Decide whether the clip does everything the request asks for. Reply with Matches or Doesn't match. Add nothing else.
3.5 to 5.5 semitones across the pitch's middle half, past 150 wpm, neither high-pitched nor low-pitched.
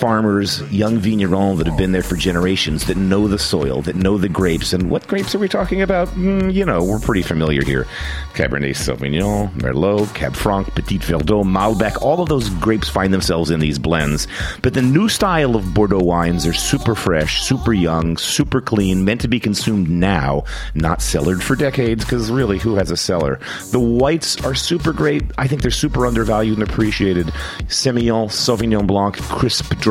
Doesn't match